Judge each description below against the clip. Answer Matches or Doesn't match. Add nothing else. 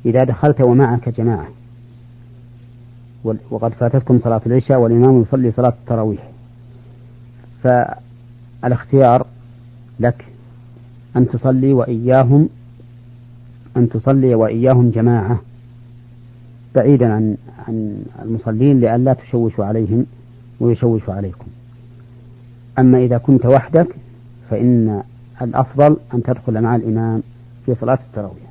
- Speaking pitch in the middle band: Doesn't match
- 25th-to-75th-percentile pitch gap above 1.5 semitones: Doesn't match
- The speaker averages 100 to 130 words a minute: Doesn't match